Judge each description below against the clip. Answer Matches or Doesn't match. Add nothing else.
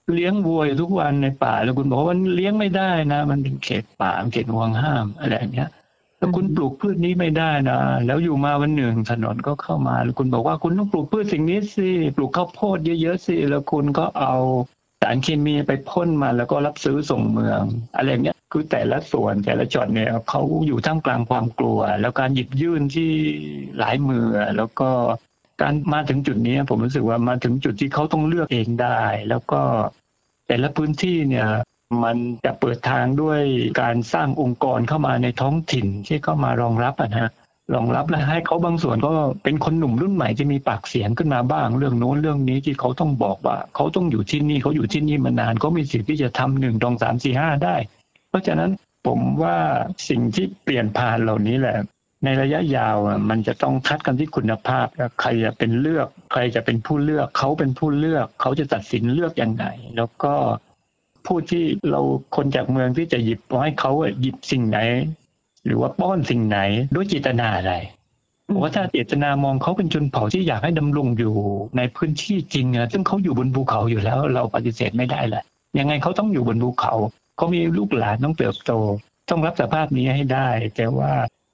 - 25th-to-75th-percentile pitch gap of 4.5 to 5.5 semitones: Matches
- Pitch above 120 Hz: Matches